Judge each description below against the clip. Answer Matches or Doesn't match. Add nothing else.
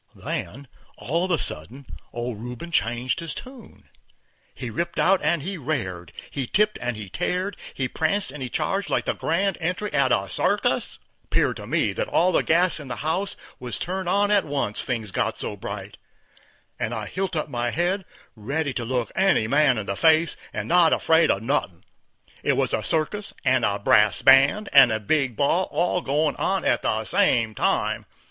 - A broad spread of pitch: Matches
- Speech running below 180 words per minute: Doesn't match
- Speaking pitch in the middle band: Matches